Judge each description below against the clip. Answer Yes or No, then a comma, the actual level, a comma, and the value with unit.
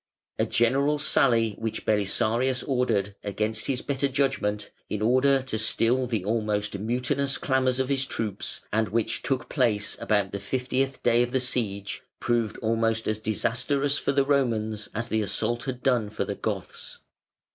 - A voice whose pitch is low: Yes, low, 120 Hz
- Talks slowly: No, average, 160 wpm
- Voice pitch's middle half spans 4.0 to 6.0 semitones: No, average, 3.4 semitones